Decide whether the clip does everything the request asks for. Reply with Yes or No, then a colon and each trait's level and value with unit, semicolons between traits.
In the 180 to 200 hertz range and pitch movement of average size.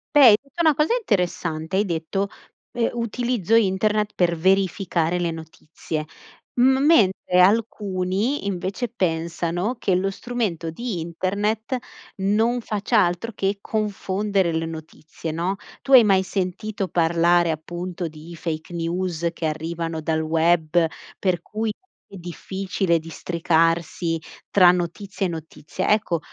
Yes: medium, 185 Hz; average, 3.9 semitones